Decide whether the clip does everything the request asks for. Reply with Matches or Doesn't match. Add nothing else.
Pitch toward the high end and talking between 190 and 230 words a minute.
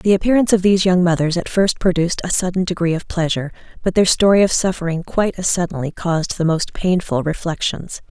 Doesn't match